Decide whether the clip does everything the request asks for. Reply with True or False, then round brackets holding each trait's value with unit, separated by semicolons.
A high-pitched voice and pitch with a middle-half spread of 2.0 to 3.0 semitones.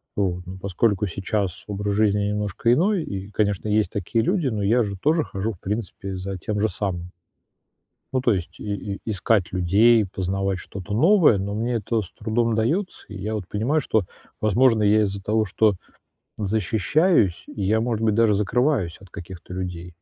False (105 Hz; 2.7 semitones)